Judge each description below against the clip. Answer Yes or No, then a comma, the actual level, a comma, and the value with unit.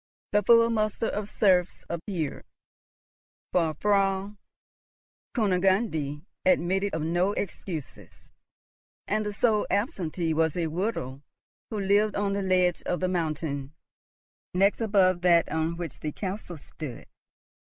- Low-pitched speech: No, medium, 185 Hz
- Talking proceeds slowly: Yes, slow, 120 wpm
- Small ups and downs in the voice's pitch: No, average, 3.9 semitones